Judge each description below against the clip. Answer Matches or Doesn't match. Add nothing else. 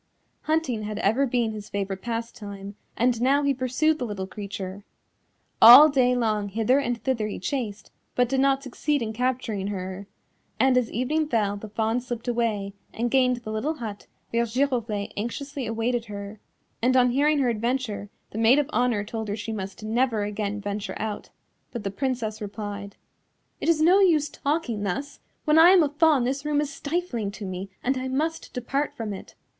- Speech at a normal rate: Matches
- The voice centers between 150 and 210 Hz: Doesn't match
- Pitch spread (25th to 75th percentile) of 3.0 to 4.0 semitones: Doesn't match